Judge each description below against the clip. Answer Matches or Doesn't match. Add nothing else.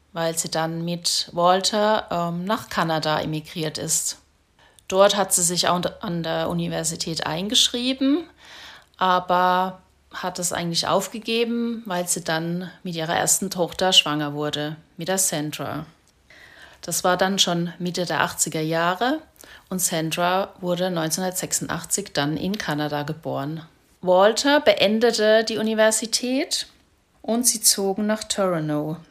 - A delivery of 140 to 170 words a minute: Doesn't match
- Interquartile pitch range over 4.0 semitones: Doesn't match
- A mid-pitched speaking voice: Matches